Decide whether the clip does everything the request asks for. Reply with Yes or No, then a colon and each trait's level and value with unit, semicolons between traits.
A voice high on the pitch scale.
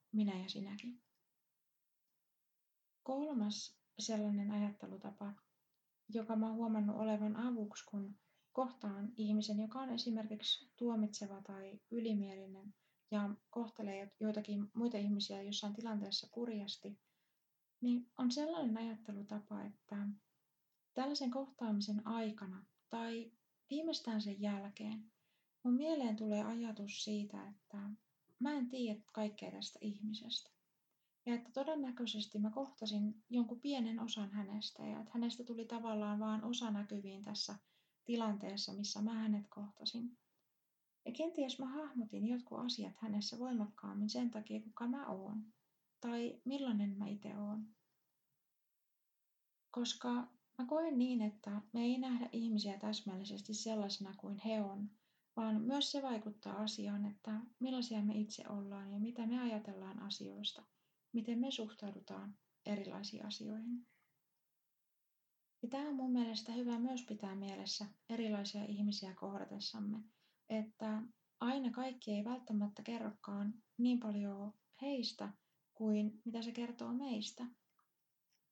Yes: high, 215 Hz